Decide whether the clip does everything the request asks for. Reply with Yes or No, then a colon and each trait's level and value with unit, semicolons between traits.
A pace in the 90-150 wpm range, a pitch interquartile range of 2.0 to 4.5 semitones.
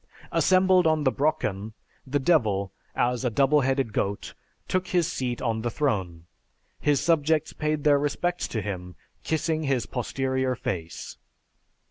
No: average, 140 wpm; wide, 5.6 semitones